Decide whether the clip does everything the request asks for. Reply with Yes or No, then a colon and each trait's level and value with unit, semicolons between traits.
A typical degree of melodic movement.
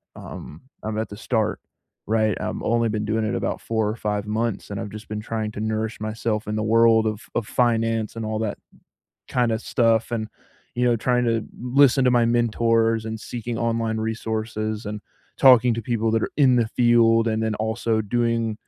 No: narrow, 1.3 semitones